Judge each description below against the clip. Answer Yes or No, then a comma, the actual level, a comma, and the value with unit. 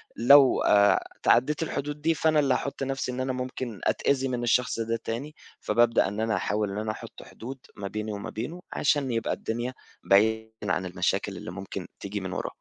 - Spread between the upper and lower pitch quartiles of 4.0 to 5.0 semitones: Yes, average, 4.3 semitones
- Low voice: Yes, low, 115 Hz